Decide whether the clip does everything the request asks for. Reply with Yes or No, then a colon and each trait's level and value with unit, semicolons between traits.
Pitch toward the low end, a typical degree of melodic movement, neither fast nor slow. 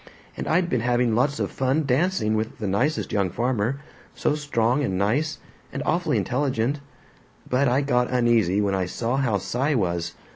Yes: low, 125 Hz; average, 4.6 semitones; average, 175 wpm